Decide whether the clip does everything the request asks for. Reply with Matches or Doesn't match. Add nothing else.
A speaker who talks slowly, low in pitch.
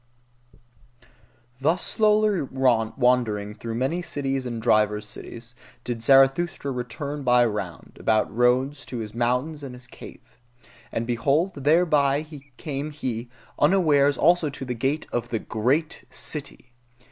Matches